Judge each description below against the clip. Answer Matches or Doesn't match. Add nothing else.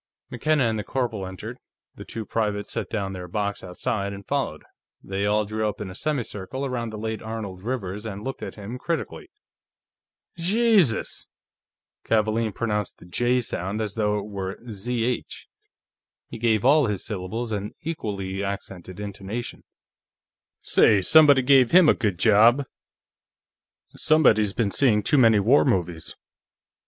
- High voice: Doesn't match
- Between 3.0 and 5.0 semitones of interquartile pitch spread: Matches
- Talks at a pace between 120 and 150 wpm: Matches